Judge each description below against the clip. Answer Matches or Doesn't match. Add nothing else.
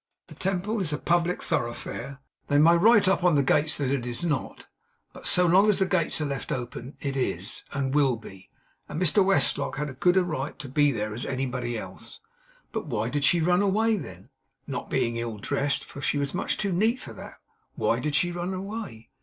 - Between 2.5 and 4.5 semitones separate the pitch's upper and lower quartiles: Doesn't match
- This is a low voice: Doesn't match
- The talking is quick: Matches